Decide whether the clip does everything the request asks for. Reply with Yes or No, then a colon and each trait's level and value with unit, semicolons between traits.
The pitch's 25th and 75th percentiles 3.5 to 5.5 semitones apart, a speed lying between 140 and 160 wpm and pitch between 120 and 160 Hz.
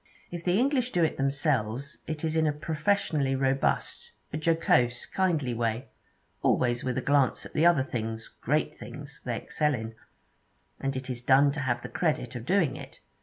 No: average, 4.2 semitones; average, 180 wpm; medium, 140 Hz